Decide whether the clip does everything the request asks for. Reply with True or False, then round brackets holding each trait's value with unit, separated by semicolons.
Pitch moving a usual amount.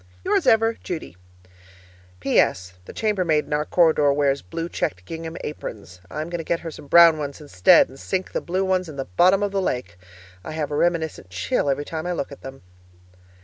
True (4.2 semitones)